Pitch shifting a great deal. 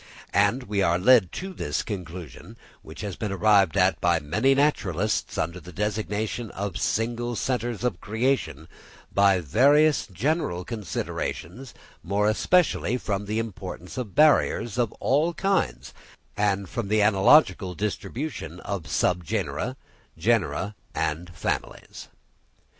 No: average, 5.0 semitones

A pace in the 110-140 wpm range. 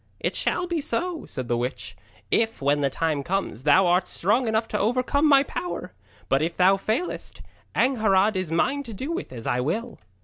No: average, 195 wpm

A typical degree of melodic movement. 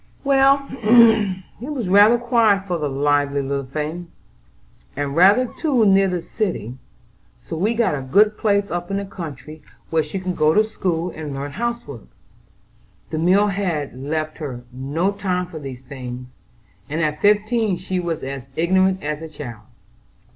No: wide, 5.8 semitones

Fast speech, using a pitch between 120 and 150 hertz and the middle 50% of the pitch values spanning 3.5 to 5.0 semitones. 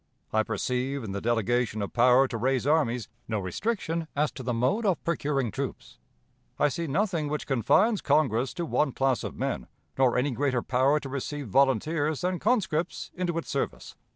No: average, 180 wpm; low, 135 Hz; average, 4.7 semitones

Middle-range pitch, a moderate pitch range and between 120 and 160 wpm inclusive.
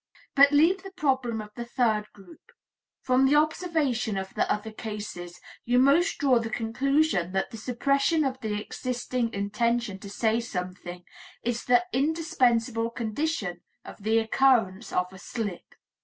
No: high, 235 Hz; average, 4.6 semitones; average, 150 wpm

